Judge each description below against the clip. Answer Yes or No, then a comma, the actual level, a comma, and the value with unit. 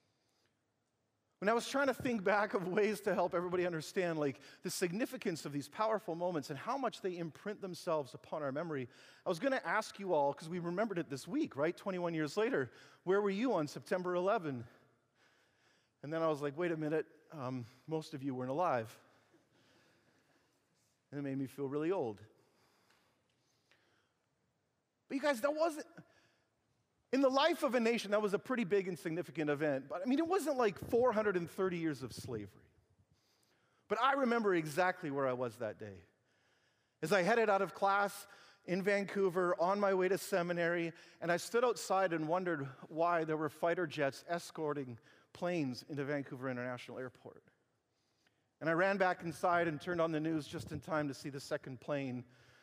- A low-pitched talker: No, medium, 170 Hz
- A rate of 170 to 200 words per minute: Yes, average, 180 wpm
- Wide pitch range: Yes, wide, 5.8 semitones